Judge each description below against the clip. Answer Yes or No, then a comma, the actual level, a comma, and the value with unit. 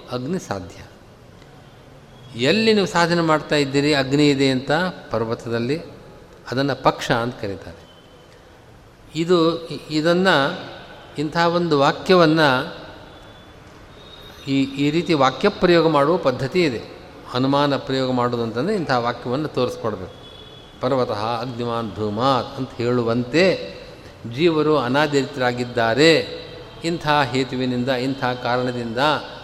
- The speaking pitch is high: No, low, 135 Hz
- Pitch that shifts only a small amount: No, average, 4.5 semitones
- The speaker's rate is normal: Yes, average, 90 wpm